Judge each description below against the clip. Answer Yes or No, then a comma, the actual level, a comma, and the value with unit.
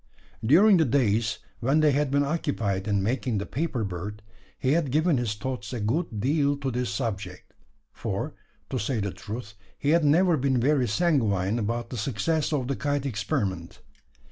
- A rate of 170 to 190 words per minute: Yes, average, 175 wpm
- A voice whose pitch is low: Yes, low, 125 Hz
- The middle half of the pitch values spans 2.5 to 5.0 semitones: No, wide, 5.5 semitones